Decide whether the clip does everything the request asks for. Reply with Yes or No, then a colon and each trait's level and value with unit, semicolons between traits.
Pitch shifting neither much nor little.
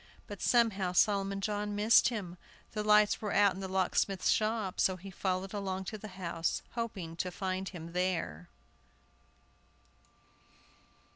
No: narrow, 2.2 semitones